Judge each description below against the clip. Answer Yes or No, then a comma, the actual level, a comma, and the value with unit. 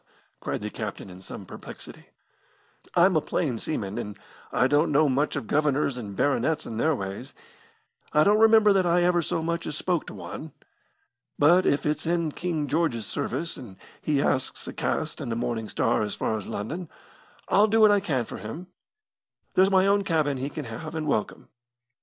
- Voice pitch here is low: No, medium, 150 Hz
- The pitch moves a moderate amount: No, wide, 6.5 semitones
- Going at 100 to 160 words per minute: No, average, 190 wpm